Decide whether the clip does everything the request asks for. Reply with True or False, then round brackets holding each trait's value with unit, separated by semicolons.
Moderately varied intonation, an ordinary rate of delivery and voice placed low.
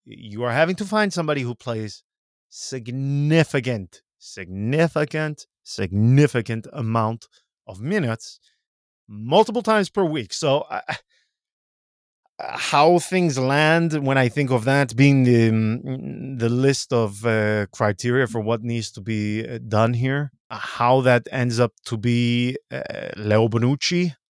False (4.2 semitones; 130 wpm; 125 Hz)